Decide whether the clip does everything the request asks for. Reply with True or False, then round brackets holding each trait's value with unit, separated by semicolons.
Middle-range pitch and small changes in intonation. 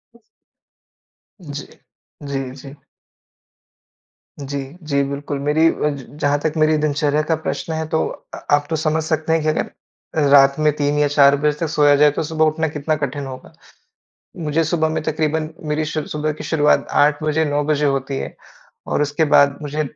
True (150 Hz; 1.5 semitones)